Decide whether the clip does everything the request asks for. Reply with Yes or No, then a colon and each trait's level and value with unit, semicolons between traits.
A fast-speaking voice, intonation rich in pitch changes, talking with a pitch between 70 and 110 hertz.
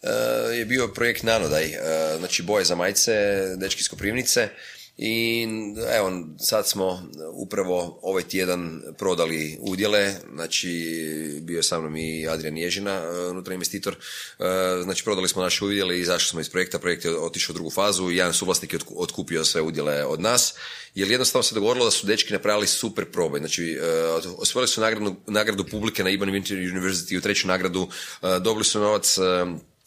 No: fast, 175 wpm; average, 3.3 semitones; very low, 95 Hz